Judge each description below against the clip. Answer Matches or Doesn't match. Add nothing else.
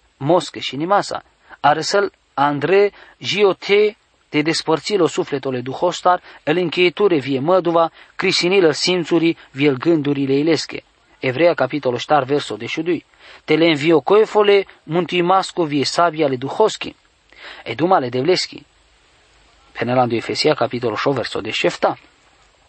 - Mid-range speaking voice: Matches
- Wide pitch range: Doesn't match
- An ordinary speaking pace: Doesn't match